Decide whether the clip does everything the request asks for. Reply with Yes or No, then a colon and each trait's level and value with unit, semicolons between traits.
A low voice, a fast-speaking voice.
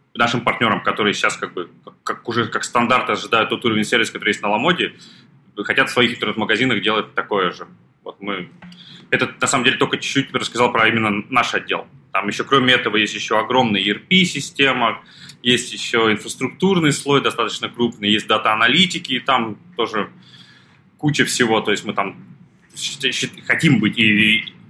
Yes: low, 125 Hz; fast, 165 wpm